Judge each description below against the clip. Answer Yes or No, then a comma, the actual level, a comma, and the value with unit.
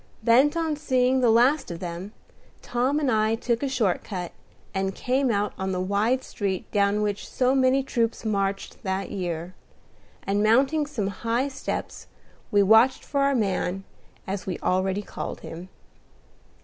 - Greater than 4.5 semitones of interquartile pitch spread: Yes, average, 5.1 semitones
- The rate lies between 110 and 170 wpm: Yes, average, 160 wpm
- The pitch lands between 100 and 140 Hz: No, high, 220 Hz